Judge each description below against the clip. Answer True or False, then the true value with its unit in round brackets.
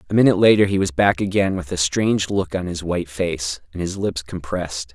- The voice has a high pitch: False (90 Hz)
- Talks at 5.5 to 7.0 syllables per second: True (5.8 syllables/s)